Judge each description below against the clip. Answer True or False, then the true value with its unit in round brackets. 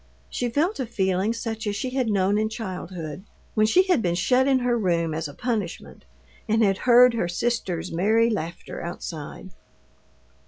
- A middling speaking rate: True (170 wpm)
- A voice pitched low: False (215 Hz)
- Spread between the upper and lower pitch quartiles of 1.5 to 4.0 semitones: False (5.0 semitones)